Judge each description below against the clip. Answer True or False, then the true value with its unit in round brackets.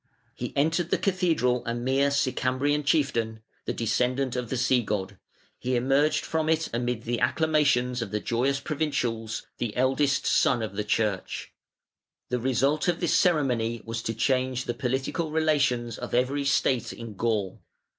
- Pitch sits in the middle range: False (125 Hz)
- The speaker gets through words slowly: False (155 wpm)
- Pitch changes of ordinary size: True (3.5 semitones)